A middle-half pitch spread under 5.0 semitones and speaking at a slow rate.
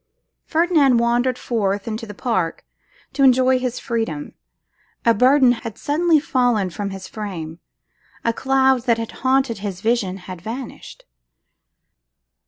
Yes: average, 4.4 semitones; slow, 130 wpm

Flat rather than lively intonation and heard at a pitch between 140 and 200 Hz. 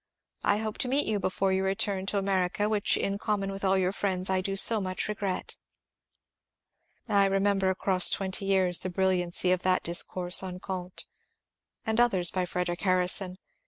Yes: narrow, 1.5 semitones; high, 190 Hz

